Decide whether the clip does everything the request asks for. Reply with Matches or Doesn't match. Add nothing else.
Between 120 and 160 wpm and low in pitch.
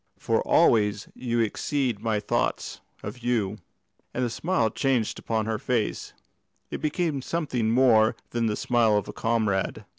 Matches